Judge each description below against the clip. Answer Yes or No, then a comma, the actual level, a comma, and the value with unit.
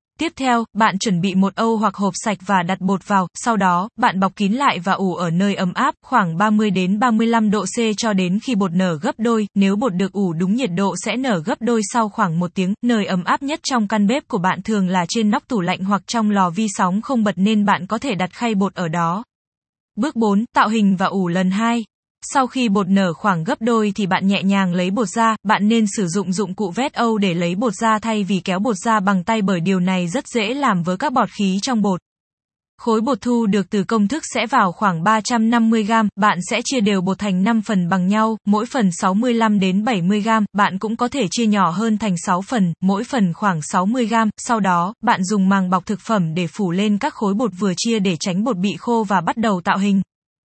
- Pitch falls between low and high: No, high, 210 Hz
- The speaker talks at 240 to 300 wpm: Yes, average, 245 wpm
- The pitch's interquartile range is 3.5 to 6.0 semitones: No, average, 3.0 semitones